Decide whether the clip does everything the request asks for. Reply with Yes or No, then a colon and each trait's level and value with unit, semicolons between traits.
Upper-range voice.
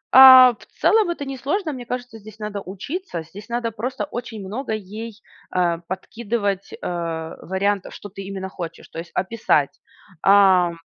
Yes: high, 210 Hz